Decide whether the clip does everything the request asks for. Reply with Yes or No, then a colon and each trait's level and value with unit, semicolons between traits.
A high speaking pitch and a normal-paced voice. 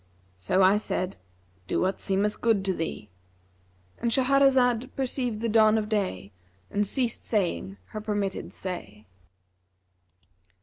No: high, 200 Hz; slow, 120 wpm